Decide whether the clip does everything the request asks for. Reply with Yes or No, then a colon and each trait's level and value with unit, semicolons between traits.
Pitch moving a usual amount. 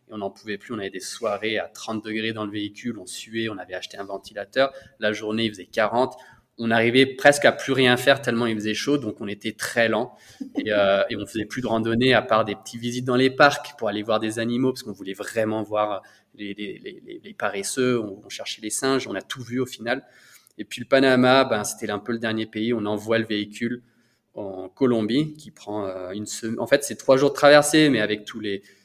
Yes: average, 3.3 semitones